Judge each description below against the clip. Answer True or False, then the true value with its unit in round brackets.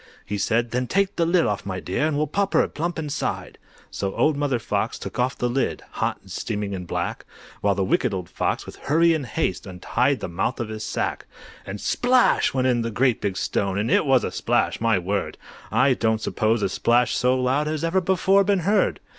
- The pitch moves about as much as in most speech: False (6.9 semitones)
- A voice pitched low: True (125 Hz)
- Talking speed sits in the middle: False (215 wpm)